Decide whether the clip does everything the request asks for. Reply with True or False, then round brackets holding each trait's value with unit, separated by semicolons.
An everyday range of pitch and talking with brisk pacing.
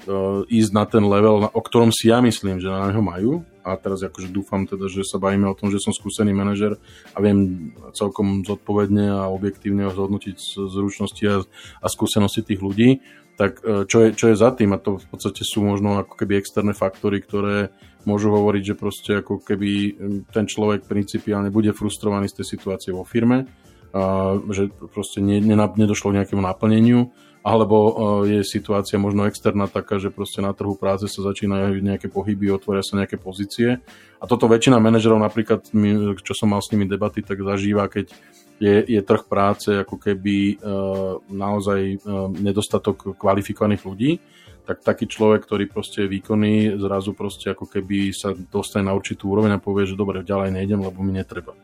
False (1.3 semitones; 175 wpm)